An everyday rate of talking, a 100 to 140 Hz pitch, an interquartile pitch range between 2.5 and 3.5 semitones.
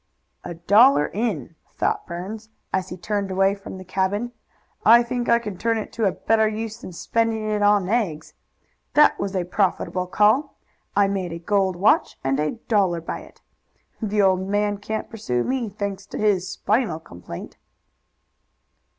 No: average, 165 wpm; high, 200 Hz; average, 3.0 semitones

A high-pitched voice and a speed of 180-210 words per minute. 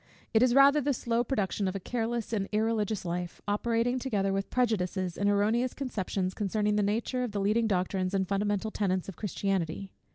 Yes: high, 205 Hz; average, 185 wpm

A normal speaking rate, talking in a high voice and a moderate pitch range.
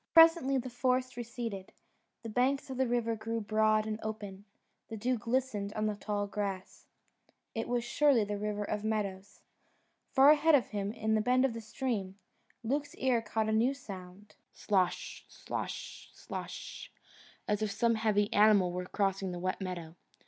Yes: average, 165 wpm; high, 220 Hz; average, 3.3 semitones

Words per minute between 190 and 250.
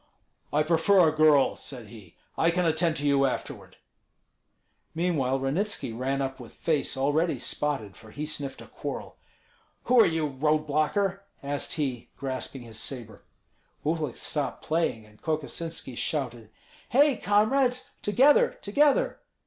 No: average, 140 wpm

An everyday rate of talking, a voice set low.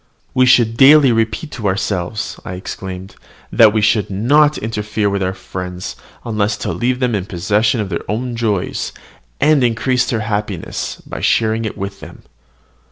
Yes: average, 165 wpm; low, 110 Hz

